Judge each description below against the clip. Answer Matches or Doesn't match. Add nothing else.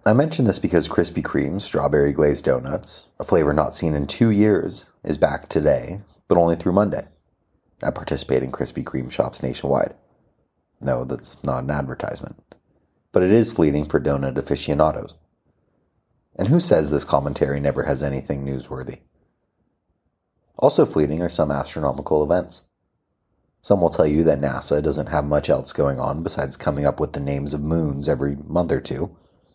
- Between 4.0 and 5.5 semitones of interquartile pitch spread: Doesn't match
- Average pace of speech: Matches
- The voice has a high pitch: Doesn't match